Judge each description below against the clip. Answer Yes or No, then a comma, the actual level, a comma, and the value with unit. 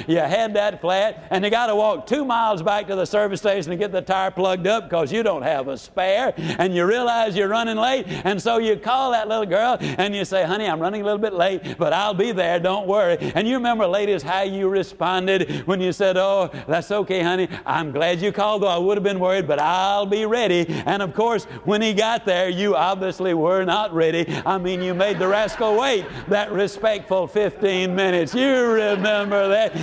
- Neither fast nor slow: No, fast, 225 wpm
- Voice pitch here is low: No, high, 200 Hz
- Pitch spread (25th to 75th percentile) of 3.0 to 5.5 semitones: No, narrow, 2.6 semitones